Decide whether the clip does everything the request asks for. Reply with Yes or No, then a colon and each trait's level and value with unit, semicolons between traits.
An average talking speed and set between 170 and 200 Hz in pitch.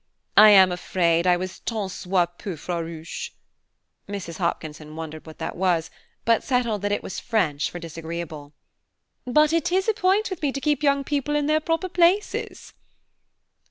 Yes: average, 165 wpm; high, 190 Hz